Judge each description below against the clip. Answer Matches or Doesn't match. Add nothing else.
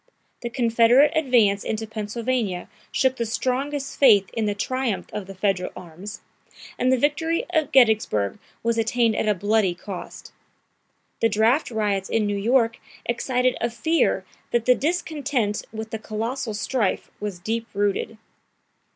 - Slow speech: Doesn't match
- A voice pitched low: Doesn't match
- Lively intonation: Doesn't match